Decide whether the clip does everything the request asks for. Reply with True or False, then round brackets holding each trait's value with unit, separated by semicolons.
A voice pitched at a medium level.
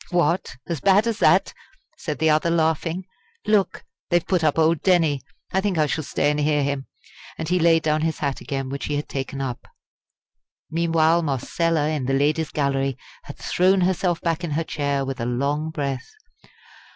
True (155 Hz)